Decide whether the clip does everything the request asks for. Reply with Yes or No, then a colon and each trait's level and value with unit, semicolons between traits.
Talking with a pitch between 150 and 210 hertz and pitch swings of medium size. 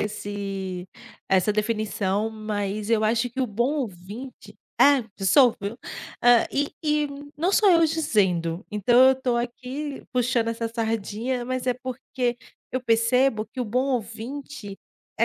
No: high, 230 Hz; average, 3.6 semitones